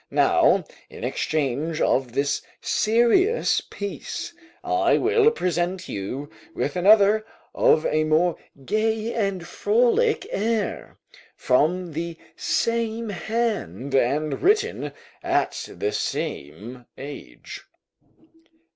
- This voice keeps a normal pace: No, slow, 95 wpm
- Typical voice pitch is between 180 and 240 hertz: Yes, medium, 185 Hz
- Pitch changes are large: Yes, wide, 7.9 semitones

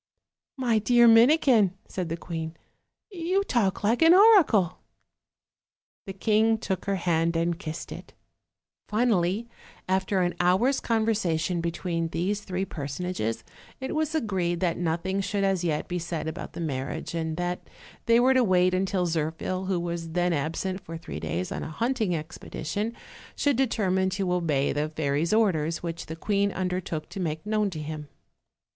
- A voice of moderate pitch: Yes, medium, 180 Hz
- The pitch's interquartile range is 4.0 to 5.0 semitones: Yes, average, 4.5 semitones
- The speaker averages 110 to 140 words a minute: No, average, 160 wpm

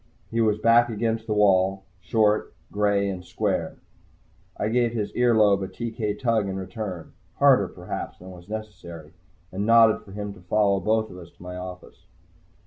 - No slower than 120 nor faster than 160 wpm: No, average, 175 wpm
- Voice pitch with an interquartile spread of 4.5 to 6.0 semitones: No, average, 3.0 semitones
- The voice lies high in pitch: No, low, 105 Hz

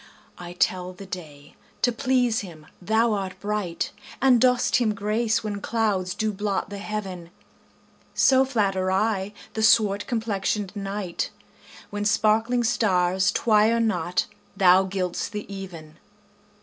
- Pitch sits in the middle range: No, high, 205 Hz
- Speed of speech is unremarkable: No, slow, 130 wpm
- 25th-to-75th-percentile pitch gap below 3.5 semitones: Yes, average, 2.9 semitones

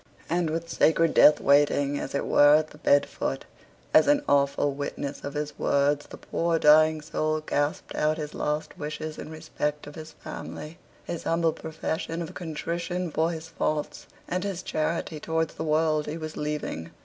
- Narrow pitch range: Yes, narrow, 1.6 semitones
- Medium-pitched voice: Yes, medium, 155 Hz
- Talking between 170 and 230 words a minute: Yes, average, 175 wpm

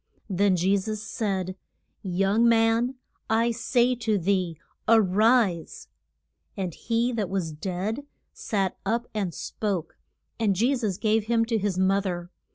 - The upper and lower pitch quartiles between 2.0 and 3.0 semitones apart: No, average, 3.4 semitones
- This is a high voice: Yes, high, 205 Hz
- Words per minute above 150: No, average, 145 wpm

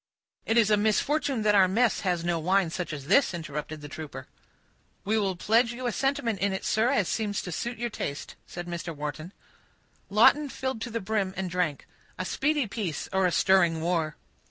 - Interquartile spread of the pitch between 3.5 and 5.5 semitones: Yes, average, 5.0 semitones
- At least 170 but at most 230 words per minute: Yes, fast, 205 wpm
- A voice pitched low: No, high, 190 Hz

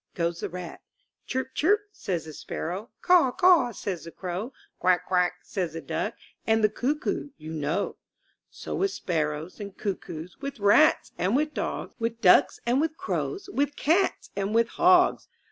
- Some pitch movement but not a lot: No, wide, 8.5 semitones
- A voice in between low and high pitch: No, high, 215 Hz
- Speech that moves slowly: No, average, 165 wpm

